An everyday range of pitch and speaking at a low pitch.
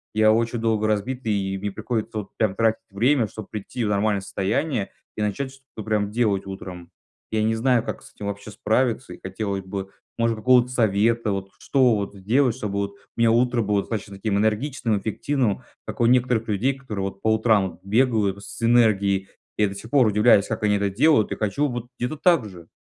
Yes: average, 3.2 semitones; low, 110 Hz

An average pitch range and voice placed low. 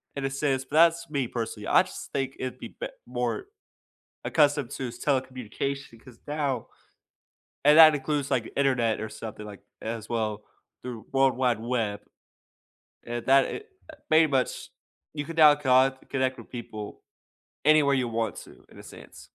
Yes: average, 3.7 semitones; low, 130 Hz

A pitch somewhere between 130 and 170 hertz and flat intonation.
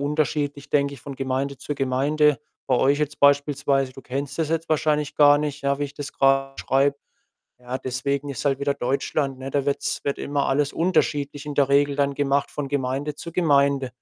Yes: medium, 140 Hz; narrow, 1.2 semitones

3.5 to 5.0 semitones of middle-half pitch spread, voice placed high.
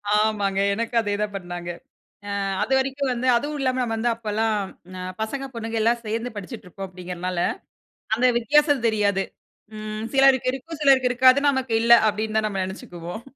Yes: average, 4.0 semitones; high, 225 Hz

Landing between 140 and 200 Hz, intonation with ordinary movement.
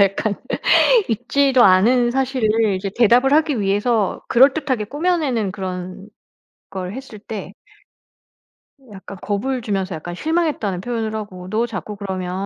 No: high, 215 Hz; average, 4.8 semitones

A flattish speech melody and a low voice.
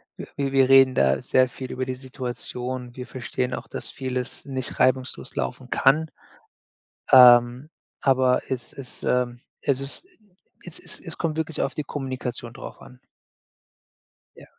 Yes: narrow, 1.3 semitones; low, 130 Hz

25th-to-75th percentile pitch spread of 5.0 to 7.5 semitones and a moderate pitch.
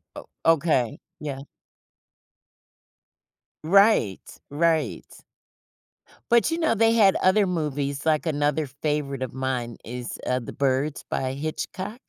Yes: wide, 5.4 semitones; medium, 150 Hz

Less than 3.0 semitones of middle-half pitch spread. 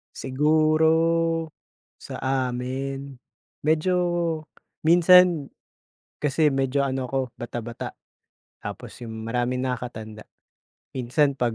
No: average, 4.0 semitones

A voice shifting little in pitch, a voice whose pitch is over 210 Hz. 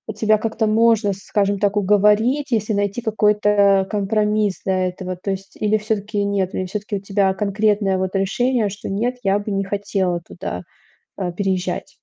No: narrow, 1.7 semitones; high, 205 Hz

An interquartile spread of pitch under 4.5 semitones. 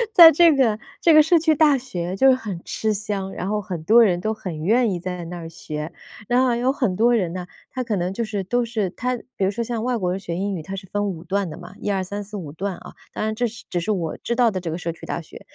No: average, 4.8 semitones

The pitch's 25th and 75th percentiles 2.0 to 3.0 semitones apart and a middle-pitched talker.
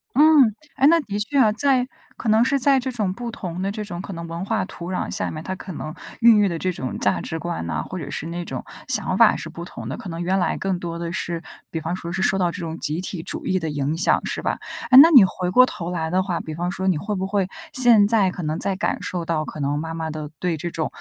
No: average, 4.1 semitones; medium, 180 Hz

